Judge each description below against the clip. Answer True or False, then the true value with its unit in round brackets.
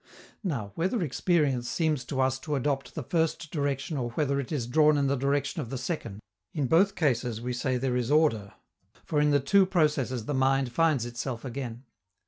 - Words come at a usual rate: True (195 wpm)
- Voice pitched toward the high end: False (140 Hz)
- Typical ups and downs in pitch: True (3.6 semitones)